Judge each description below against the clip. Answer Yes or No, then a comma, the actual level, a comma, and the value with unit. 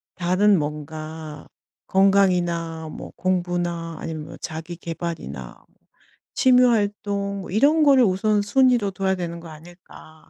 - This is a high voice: No, medium, 175 Hz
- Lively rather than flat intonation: No, average, 3.8 semitones